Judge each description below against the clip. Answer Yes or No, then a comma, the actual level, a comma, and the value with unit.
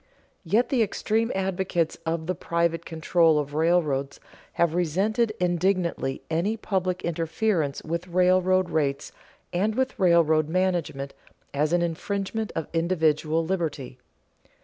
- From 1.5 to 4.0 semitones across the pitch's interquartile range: Yes, average, 2.9 semitones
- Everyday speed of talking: No, slow, 120 wpm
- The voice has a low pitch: No, medium, 170 Hz